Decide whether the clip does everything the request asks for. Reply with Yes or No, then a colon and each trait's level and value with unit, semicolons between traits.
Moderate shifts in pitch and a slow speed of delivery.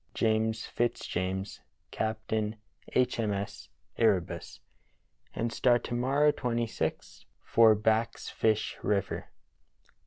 No: narrow, 1.9 semitones; slow, 95 wpm